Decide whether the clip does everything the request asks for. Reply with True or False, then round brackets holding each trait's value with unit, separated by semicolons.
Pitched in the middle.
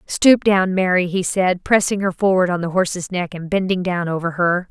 True (180 Hz)